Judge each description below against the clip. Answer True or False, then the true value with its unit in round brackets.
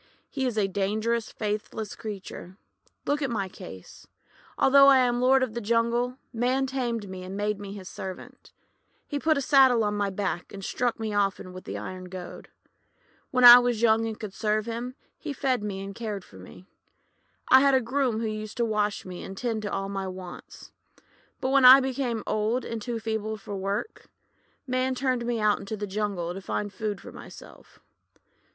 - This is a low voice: False (220 Hz)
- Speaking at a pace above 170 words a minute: True (195 wpm)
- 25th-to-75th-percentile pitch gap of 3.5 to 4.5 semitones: True (3.8 semitones)